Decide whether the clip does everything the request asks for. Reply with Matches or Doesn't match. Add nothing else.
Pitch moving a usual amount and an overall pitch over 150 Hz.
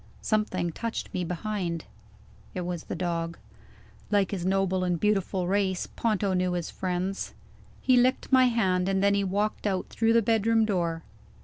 Matches